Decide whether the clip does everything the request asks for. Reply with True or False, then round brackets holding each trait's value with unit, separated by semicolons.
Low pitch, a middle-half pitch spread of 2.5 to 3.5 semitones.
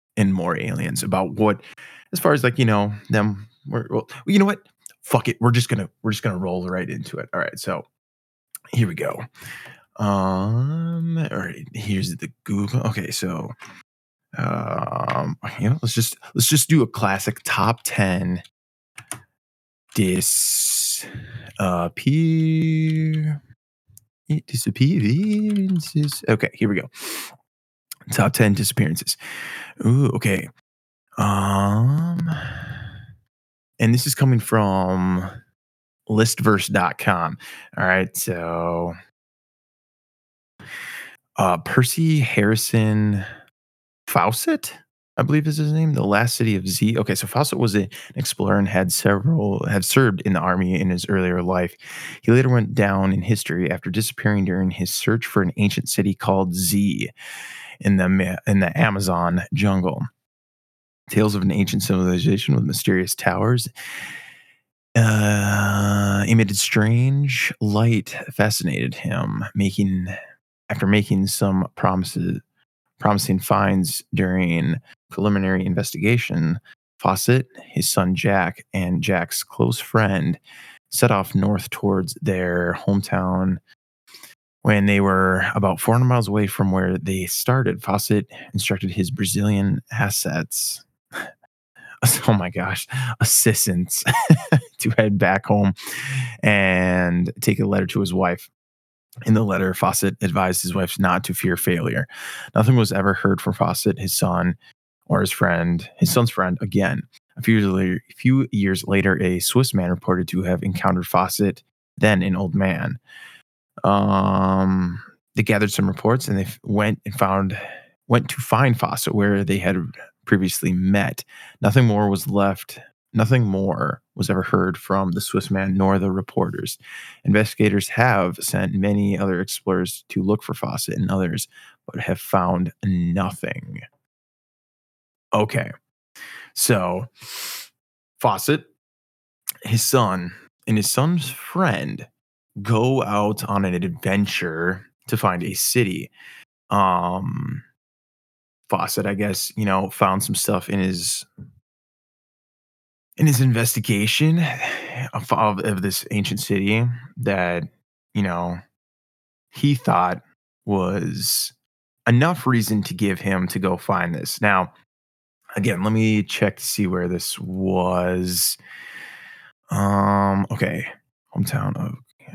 False (100 Hz; 4.0 semitones)